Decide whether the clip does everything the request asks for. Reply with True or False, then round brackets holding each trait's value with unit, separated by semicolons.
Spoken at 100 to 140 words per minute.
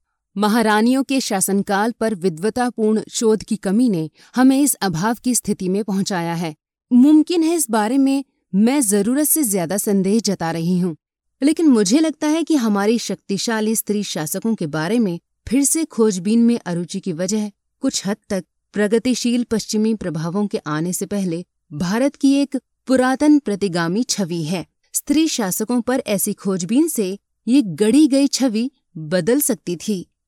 False (155 wpm)